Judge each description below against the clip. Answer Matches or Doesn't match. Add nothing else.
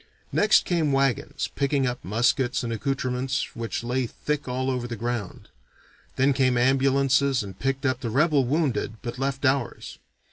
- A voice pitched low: Matches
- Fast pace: Doesn't match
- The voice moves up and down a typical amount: Doesn't match